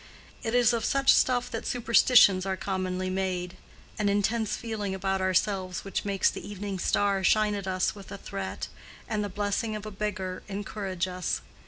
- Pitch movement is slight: Yes, narrow, 2.3 semitones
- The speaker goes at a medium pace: Yes, average, 175 wpm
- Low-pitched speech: No, high, 200 Hz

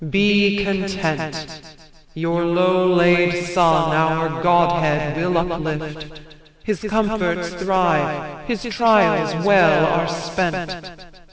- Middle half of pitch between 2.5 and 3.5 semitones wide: Yes, average, 2.8 semitones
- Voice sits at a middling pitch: Yes, medium, 175 Hz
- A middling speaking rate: No, slow, 95 wpm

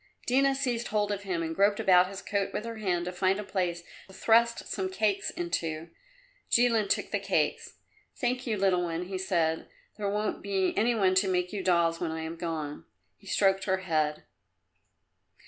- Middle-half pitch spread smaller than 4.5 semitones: Yes, average, 3.2 semitones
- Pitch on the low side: No, high, 190 Hz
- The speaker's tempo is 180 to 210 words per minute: Yes, average, 190 wpm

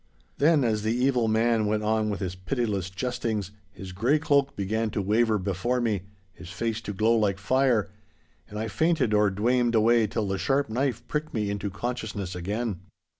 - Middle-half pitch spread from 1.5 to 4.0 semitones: Yes, average, 3.2 semitones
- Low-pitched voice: Yes, low, 110 Hz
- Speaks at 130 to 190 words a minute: Yes, average, 180 wpm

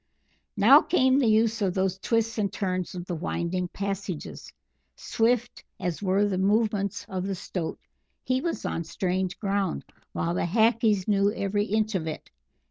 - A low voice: No, high, 200 Hz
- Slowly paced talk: No, average, 160 wpm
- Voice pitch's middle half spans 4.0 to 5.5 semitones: No, average, 3.1 semitones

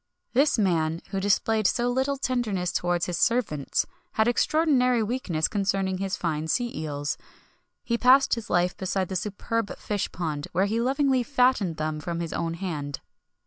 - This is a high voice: Yes, high, 195 Hz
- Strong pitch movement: Yes, wide, 6.3 semitones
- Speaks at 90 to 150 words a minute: No, average, 175 wpm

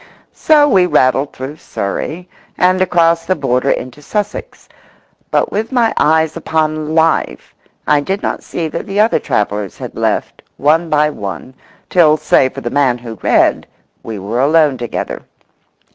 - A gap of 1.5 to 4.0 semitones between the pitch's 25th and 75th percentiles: No, average, 5.2 semitones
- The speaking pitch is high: No, medium, 155 Hz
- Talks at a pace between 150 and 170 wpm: Yes, average, 155 wpm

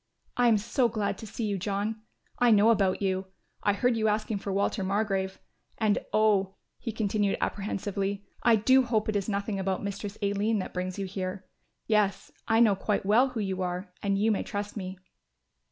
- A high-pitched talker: Yes, high, 205 Hz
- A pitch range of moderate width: No, narrow, 1.9 semitones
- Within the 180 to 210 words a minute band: Yes, average, 190 wpm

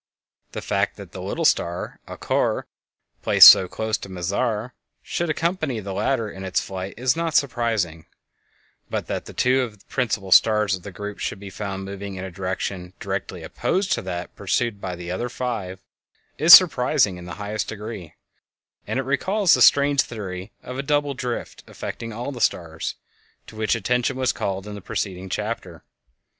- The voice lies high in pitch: No, low, 105 Hz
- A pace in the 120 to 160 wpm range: No, average, 175 wpm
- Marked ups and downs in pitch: No, average, 5.0 semitones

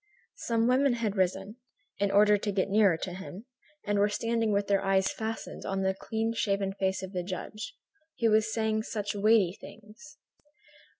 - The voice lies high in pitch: Yes, high, 205 Hz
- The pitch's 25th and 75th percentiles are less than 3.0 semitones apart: Yes, narrow, 2.4 semitones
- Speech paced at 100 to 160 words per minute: No, average, 175 wpm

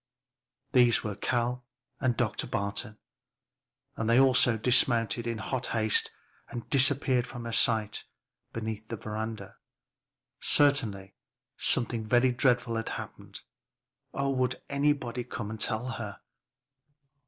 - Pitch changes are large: No, narrow, 2.5 semitones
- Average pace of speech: No, slow, 120 wpm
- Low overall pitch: Yes, low, 120 Hz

